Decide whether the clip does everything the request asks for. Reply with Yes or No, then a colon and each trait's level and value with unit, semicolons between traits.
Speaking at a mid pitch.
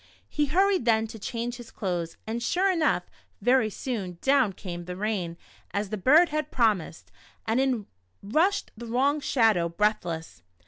No: high, 225 Hz